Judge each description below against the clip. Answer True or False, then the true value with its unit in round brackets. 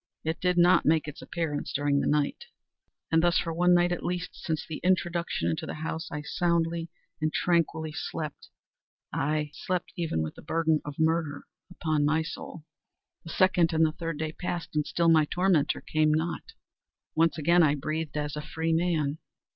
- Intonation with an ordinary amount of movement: False (2.0 semitones)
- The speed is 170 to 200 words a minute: True (180 wpm)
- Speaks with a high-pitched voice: False (160 Hz)